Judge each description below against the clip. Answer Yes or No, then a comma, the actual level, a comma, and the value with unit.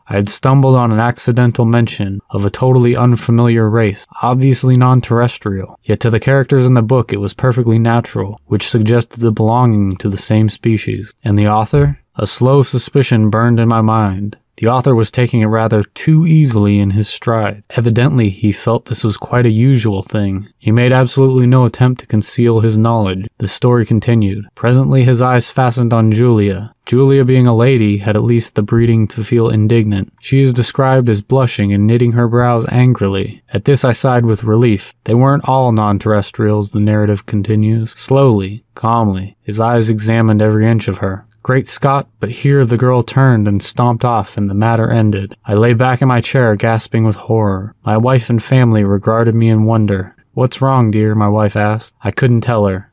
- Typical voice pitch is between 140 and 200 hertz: No, low, 115 Hz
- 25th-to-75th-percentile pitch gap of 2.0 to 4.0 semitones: Yes, average, 2.8 semitones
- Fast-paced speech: No, average, 190 wpm